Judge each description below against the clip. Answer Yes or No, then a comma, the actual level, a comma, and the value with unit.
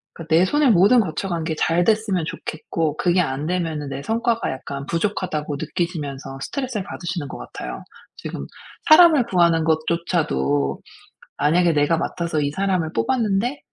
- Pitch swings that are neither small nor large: Yes, average, 4.6 semitones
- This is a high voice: No, medium, 170 Hz